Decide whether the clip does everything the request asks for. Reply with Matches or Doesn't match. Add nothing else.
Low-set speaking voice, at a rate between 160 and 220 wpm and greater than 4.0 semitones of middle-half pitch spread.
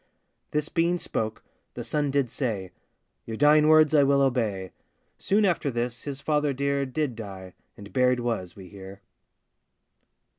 Doesn't match